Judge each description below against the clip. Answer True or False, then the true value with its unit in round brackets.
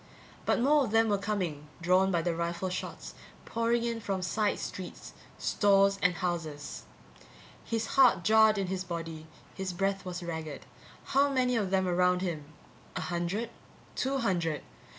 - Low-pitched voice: False (190 Hz)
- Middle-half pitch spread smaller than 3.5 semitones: False (4.1 semitones)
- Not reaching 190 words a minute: True (155 wpm)